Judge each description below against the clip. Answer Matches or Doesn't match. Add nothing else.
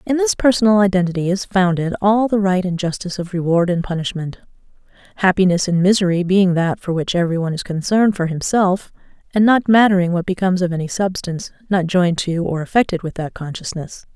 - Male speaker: Doesn't match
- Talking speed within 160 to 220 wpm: Matches